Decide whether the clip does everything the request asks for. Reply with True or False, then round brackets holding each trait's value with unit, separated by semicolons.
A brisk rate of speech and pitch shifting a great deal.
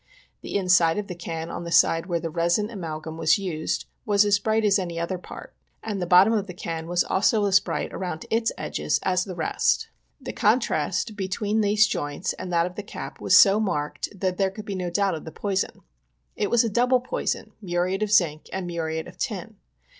False (215 wpm; 3.4 semitones)